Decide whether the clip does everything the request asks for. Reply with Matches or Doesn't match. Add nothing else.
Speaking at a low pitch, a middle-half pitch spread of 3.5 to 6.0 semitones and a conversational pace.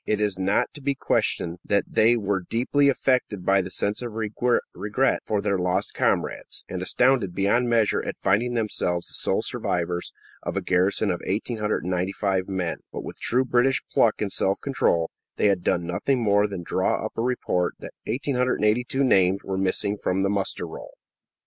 Matches